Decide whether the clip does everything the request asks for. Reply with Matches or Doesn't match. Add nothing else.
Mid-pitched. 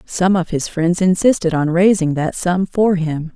Matches